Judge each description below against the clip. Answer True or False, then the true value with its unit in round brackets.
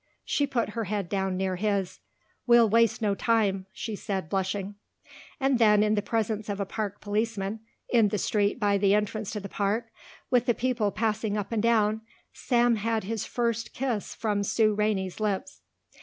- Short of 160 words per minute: False (180 wpm)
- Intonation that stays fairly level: True (2.2 semitones)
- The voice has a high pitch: True (210 Hz)